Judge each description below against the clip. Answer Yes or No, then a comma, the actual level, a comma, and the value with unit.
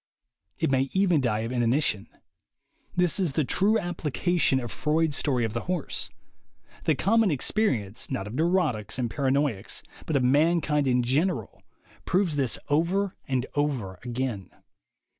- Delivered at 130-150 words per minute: Yes, average, 140 wpm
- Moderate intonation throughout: No, wide, 5.8 semitones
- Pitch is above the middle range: No, medium, 140 Hz